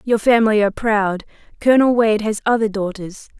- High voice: Yes, high, 215 Hz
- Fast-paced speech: No, average, 160 wpm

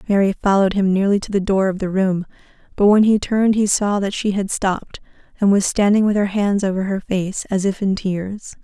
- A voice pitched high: Yes, high, 195 Hz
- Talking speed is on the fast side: Yes, fast, 230 wpm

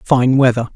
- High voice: No, low, 125 Hz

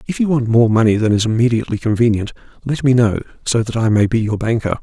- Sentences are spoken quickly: Yes, fast, 235 wpm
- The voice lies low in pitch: Yes, low, 115 Hz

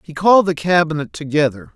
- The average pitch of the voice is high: No, medium, 160 Hz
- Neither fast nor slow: Yes, average, 170 wpm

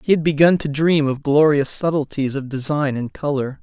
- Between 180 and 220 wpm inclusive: Yes, average, 200 wpm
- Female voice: No, male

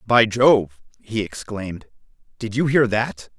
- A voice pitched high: No, low, 110 Hz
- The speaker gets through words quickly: No, average, 140 wpm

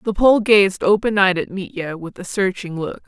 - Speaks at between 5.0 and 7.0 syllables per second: No, 4.7 syllables/s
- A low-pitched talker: No, high, 195 Hz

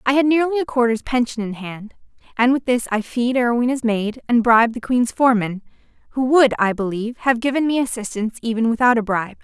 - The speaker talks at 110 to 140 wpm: No, average, 195 wpm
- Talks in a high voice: Yes, high, 240 Hz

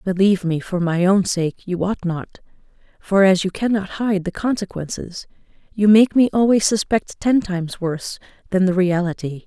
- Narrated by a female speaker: Yes, female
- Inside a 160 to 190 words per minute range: Yes, average, 170 wpm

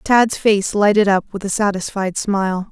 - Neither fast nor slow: Yes, average, 175 wpm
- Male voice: No, female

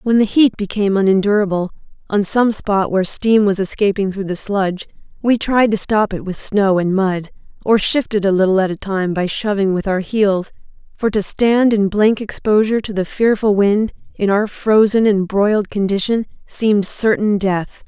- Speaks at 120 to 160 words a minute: No, average, 185 wpm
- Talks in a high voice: Yes, high, 205 Hz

